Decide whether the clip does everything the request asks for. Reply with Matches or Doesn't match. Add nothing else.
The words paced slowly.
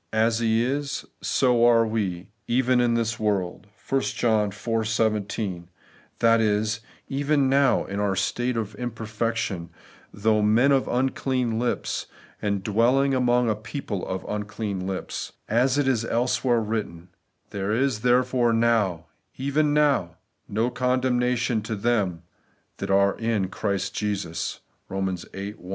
Doesn't match